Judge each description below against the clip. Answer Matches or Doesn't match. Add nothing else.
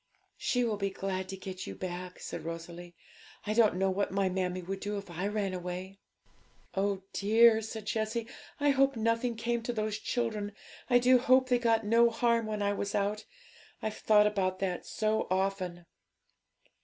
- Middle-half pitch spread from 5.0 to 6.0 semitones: Doesn't match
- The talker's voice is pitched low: Doesn't match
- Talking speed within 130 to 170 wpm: Doesn't match